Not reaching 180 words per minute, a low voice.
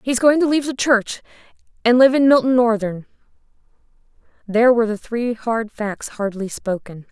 No: average, 160 wpm; high, 235 Hz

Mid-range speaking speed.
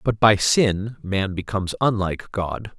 Yes: average, 150 wpm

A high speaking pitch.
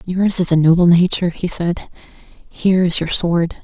No: medium, 175 Hz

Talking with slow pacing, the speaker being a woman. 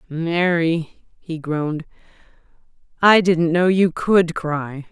Yes: slow, 110 wpm; female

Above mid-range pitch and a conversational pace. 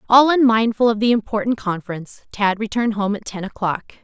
Yes: high, 215 Hz; average, 180 wpm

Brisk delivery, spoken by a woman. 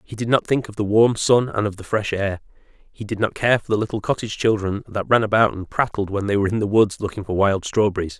No: fast, 270 wpm; male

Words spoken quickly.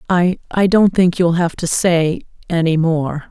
No: average, 145 wpm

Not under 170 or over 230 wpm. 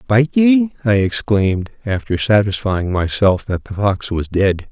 No: average, 155 wpm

